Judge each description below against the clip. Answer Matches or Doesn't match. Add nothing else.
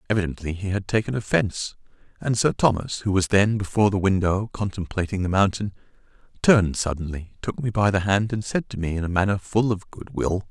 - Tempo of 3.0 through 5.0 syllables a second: Doesn't match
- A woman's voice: Doesn't match